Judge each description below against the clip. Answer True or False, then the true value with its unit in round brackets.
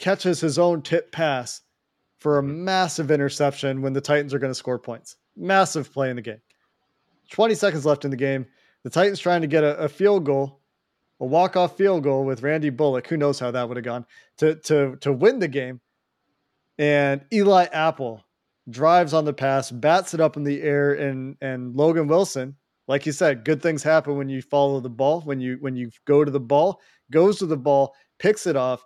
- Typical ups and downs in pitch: True (3.3 semitones)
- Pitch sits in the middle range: True (145 Hz)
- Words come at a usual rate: False (210 wpm)